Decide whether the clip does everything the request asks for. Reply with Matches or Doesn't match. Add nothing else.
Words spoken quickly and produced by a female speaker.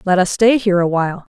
Matches